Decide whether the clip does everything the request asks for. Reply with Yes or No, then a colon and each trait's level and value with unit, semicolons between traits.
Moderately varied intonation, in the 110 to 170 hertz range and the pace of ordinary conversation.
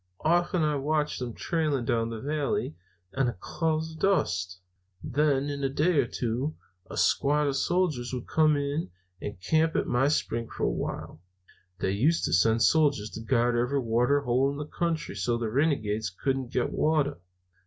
Yes: average, 4.7 semitones; medium, 140 Hz; average, 180 wpm